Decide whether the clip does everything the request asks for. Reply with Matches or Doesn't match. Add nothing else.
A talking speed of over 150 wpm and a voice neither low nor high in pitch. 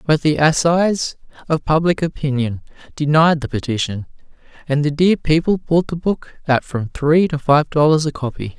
Matches